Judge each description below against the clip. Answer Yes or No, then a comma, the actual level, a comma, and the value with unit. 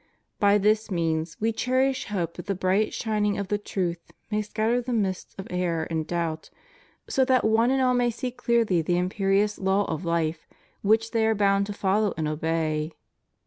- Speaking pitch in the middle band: No, high, 200 Hz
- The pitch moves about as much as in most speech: Yes, average, 4.4 semitones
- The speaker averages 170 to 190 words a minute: Yes, average, 185 wpm